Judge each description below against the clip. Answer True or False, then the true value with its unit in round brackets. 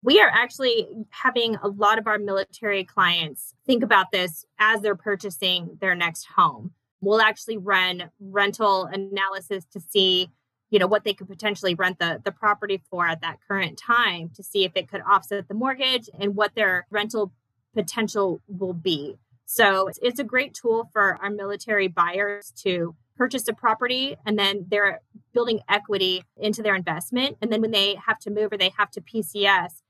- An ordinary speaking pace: True (180 wpm)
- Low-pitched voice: False (200 Hz)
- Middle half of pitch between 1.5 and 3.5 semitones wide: True (2.5 semitones)